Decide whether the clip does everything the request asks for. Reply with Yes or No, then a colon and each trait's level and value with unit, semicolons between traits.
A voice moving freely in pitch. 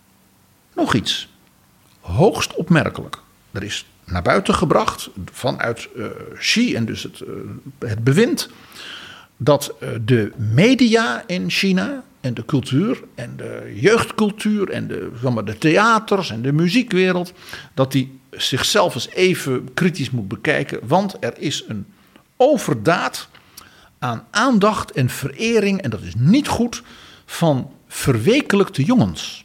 Yes: wide, 8.9 semitones